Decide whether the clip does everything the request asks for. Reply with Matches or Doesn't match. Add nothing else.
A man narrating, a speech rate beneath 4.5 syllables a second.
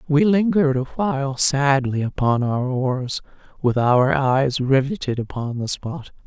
Doesn't match